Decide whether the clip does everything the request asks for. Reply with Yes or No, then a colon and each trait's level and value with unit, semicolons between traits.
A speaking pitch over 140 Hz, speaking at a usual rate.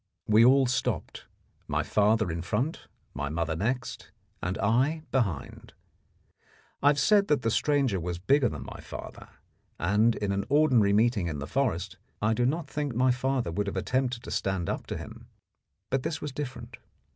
No: low, 120 Hz; average, 175 wpm